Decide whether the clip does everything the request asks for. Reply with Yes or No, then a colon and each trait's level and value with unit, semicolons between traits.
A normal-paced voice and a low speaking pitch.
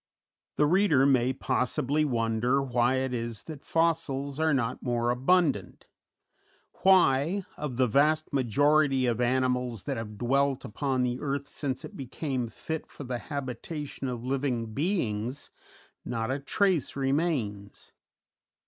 No: slow, 130 wpm; low, 130 Hz